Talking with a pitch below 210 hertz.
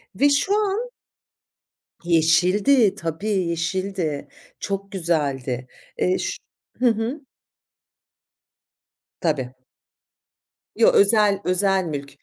Yes: high, 190 Hz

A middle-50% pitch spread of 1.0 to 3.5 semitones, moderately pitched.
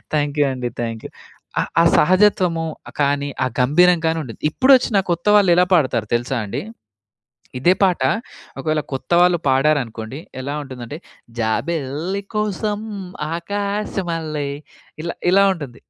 No: average, 5.3 semitones; medium, 155 Hz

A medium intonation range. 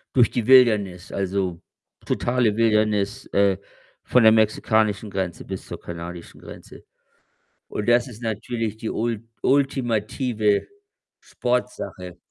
Yes: average, 3.3 semitones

